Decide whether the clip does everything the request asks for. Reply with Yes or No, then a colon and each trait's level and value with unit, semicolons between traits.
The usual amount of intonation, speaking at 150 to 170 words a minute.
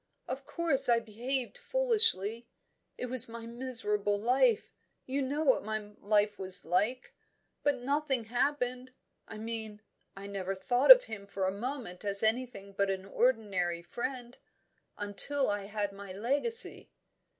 No: average, 4.4 semitones; average, 140 wpm